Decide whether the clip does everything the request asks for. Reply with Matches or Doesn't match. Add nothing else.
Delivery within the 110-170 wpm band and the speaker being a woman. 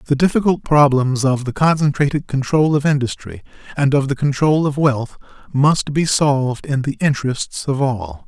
Doesn't match